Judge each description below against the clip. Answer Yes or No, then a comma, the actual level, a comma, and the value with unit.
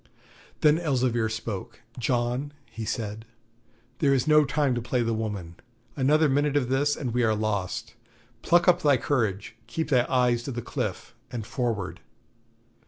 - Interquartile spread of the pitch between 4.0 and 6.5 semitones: Yes, average, 4.5 semitones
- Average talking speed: Yes, average, 160 wpm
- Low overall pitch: Yes, low, 125 Hz